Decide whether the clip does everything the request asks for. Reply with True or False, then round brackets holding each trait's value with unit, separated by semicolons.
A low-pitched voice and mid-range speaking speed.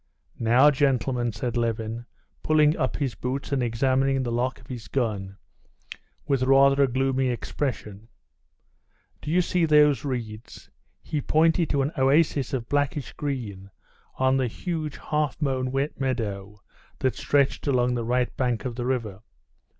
True (130 Hz; 150 wpm)